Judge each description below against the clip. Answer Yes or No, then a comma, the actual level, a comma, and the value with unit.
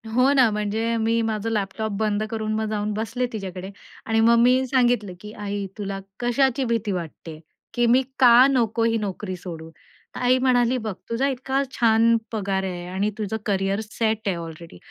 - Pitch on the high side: Yes, high, 220 Hz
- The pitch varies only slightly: No, average, 3.1 semitones